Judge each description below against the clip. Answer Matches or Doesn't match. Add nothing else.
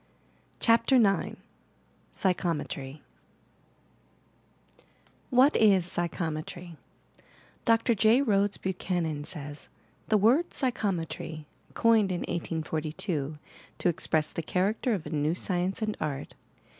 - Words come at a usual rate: Doesn't match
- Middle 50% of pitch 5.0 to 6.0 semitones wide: Matches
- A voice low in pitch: Doesn't match